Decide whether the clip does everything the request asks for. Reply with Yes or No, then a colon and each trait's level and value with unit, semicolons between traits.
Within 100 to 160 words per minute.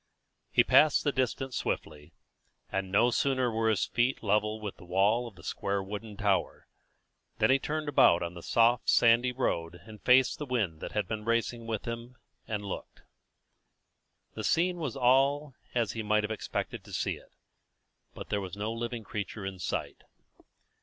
No: average, 175 wpm